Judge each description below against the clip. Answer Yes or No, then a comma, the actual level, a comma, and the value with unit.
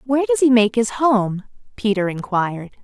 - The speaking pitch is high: Yes, high, 215 Hz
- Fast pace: No, average, 170 wpm